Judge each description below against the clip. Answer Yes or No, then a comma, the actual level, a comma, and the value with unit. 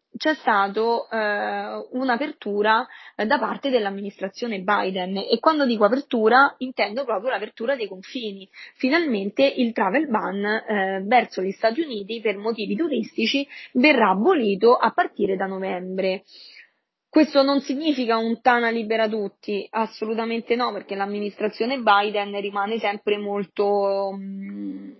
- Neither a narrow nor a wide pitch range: Yes, average, 3.8 semitones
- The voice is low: No, high, 220 Hz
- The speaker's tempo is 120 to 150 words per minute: Yes, average, 125 wpm